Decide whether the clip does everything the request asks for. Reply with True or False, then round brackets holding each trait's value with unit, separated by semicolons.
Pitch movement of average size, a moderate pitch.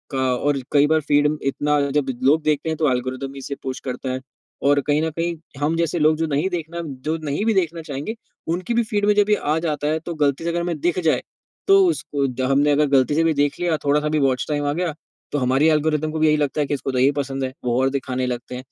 True (3.0 semitones; 150 Hz)